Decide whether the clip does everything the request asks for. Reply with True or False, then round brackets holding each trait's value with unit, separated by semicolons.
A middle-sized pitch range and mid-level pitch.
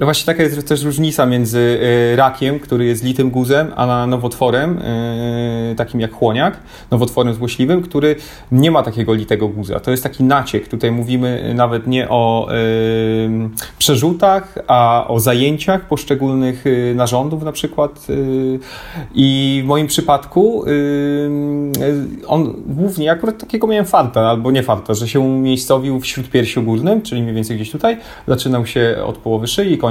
False (3.7 semitones; 130 Hz)